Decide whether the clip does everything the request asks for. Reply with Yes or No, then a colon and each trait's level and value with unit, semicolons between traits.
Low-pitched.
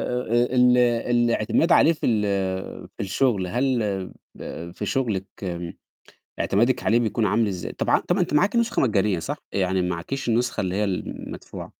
Yes: low, 115 Hz